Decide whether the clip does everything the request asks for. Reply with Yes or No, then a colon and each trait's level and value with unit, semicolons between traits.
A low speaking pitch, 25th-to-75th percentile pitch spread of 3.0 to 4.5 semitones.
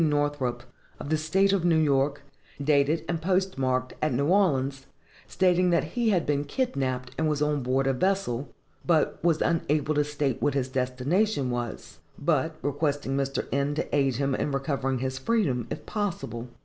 No: medium, 145 Hz; average, 3.6 semitones